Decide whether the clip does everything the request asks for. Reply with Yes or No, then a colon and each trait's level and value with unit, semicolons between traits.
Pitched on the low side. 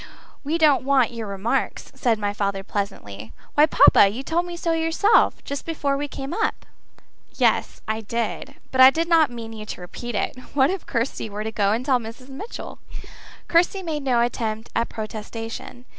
No: high, 245 Hz